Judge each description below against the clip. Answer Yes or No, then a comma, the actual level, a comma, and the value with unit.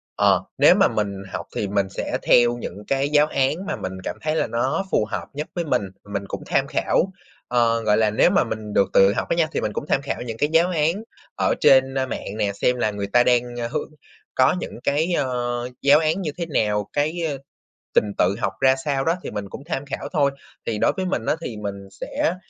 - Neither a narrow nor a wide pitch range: No, wide, 6.0 semitones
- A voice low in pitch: Yes, low, 125 Hz